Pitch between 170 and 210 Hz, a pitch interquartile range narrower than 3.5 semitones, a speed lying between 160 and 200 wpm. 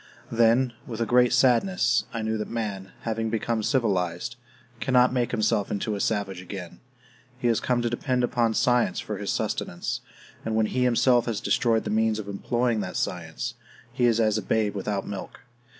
No: low, 115 Hz; average, 2.8 semitones; average, 180 wpm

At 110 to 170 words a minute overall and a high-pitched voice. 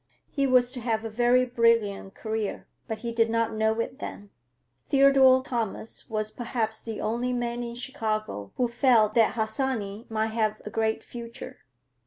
Yes: average, 165 wpm; high, 230 Hz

